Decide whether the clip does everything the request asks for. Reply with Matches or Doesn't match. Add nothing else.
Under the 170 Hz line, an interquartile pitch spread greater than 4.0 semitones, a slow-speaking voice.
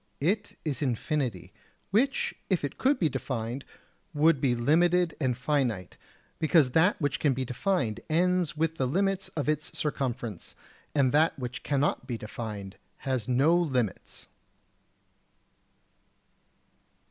Matches